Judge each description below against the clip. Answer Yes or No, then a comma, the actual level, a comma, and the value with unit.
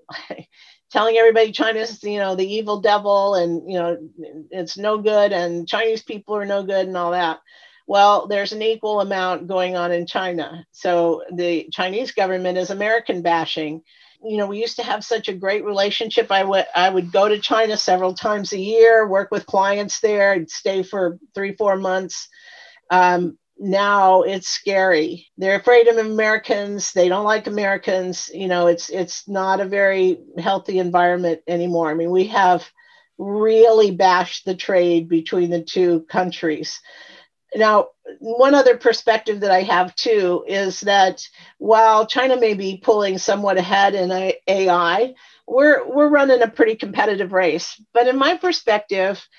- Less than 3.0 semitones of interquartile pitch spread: No, average, 3.3 semitones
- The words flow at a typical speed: Yes, average, 165 wpm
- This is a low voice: No, high, 195 Hz